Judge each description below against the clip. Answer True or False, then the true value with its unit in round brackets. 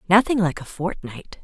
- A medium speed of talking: True (165 wpm)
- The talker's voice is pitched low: False (190 Hz)